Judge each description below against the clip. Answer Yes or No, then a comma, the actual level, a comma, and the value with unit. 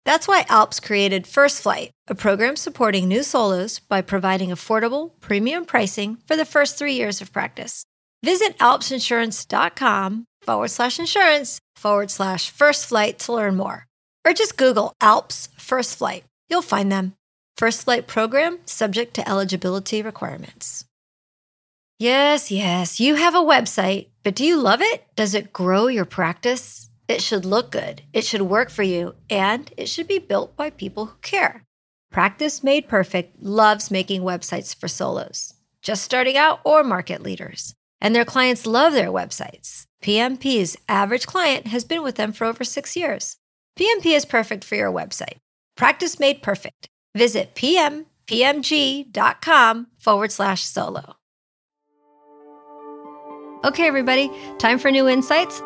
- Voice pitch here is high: Yes, high, 225 Hz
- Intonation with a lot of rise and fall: Yes, wide, 6.3 semitones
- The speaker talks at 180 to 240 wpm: No, average, 145 wpm